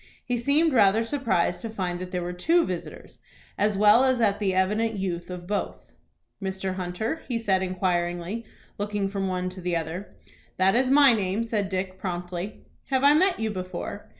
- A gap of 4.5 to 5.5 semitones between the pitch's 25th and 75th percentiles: No, average, 3.8 semitones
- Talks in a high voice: Yes, high, 195 Hz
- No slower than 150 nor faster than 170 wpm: No, average, 180 wpm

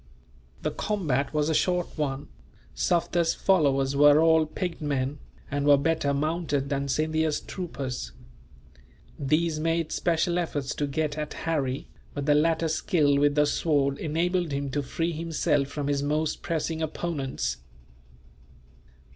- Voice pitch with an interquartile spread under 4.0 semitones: Yes, narrow, 2.6 semitones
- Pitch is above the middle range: No, medium, 150 Hz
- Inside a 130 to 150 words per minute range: Yes, average, 140 wpm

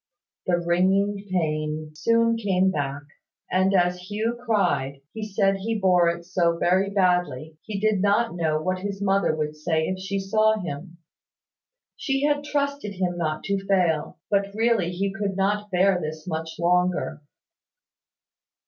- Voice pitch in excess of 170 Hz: Yes, medium, 185 Hz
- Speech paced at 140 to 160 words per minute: Yes, average, 150 wpm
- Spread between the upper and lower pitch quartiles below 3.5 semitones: Yes, average, 3.1 semitones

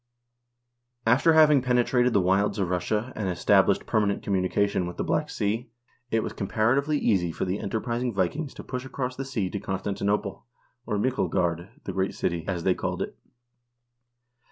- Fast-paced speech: No, average, 170 wpm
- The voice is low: Yes, low, 105 Hz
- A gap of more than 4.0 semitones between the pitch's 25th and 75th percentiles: Yes, average, 4.8 semitones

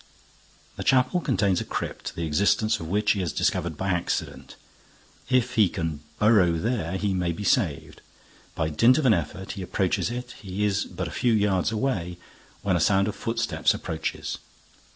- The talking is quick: No, average, 175 wpm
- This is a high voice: No, low, 100 Hz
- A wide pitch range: No, average, 4.3 semitones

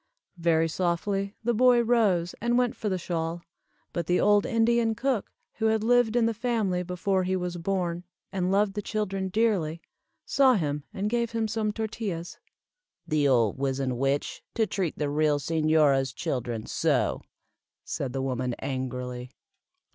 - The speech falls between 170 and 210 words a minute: No, average, 155 wpm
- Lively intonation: Yes, wide, 6.5 semitones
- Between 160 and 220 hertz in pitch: Yes, medium, 185 Hz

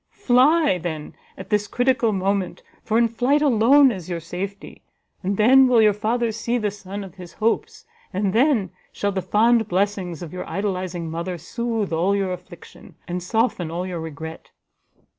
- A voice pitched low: No, high, 200 Hz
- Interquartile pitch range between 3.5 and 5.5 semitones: Yes, average, 4.3 semitones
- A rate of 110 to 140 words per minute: No, average, 170 wpm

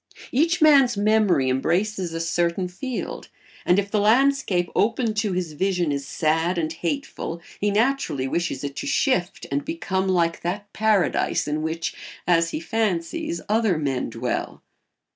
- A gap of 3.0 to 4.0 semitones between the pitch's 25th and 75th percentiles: No, average, 4.6 semitones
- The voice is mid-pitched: Yes, medium, 180 Hz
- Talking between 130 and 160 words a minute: Yes, average, 150 wpm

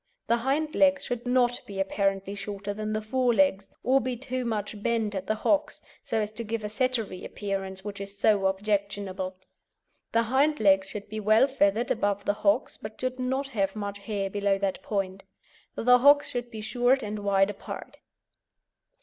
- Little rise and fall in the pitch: No, average, 3.6 semitones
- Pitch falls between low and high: No, high, 215 Hz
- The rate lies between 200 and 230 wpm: No, average, 185 wpm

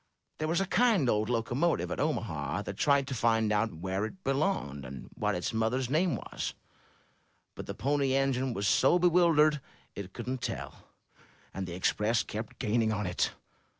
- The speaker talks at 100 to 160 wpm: No, average, 170 wpm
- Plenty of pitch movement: Yes, wide, 5.9 semitones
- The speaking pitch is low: Yes, low, 120 Hz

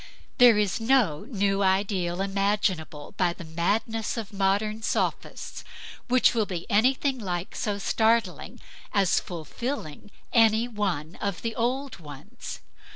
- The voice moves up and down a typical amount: Yes, average, 3.9 semitones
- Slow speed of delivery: Yes, slow, 125 wpm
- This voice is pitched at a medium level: No, high, 205 Hz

